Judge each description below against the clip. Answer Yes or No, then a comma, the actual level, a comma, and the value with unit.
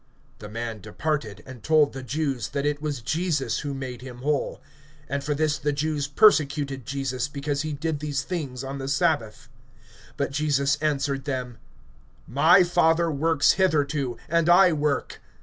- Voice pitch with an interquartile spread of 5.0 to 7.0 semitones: No, narrow, 2.5 semitones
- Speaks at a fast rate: No, average, 160 wpm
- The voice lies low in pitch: No, medium, 145 Hz